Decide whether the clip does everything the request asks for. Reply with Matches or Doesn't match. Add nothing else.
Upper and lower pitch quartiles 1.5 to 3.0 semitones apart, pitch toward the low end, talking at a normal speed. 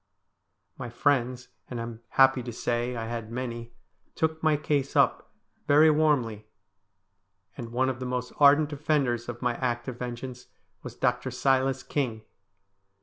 Matches